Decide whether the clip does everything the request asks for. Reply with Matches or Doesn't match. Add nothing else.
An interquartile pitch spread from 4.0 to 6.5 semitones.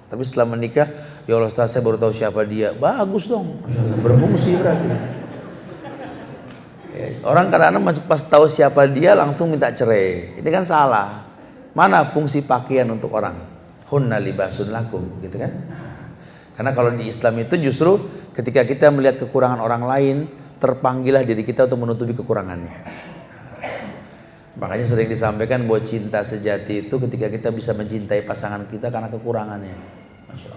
Matches